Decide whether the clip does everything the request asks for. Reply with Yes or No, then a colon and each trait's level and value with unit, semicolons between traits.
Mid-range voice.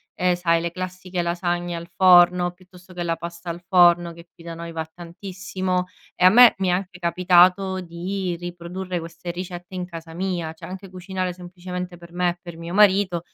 Yes: medium, 180 Hz